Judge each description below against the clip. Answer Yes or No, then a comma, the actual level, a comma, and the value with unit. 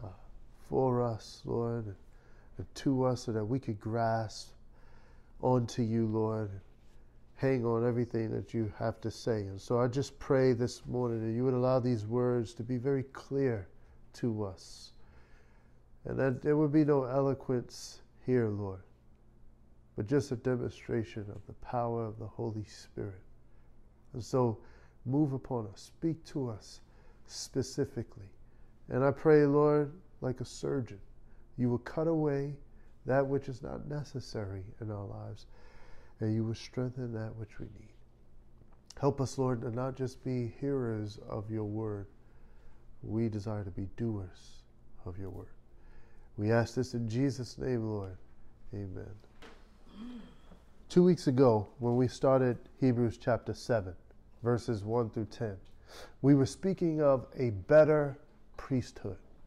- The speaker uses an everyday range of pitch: Yes, average, 3.3 semitones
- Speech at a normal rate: Yes, average, 145 wpm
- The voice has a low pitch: Yes, low, 120 Hz